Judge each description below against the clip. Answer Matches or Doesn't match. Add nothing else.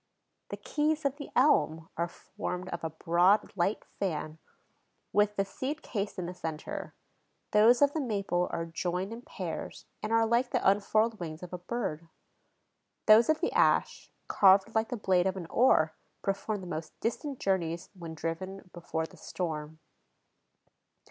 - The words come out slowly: Doesn't match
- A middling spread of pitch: Matches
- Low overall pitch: Doesn't match